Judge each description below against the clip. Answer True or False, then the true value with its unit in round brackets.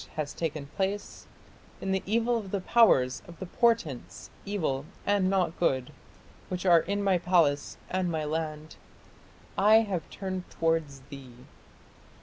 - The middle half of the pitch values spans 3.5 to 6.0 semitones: True (4.4 semitones)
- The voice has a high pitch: False (180 Hz)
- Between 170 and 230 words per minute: False (140 wpm)